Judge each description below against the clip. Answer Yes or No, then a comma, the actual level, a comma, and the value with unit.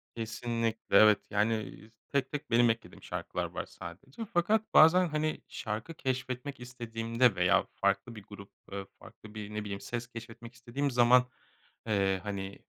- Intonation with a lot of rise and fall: No, average, 3.2 semitones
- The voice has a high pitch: No, low, 115 Hz